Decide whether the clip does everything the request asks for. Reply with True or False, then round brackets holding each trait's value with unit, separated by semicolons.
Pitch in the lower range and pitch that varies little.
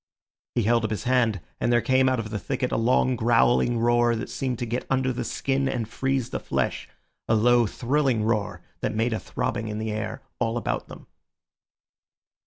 True (120 Hz; 2.2 semitones)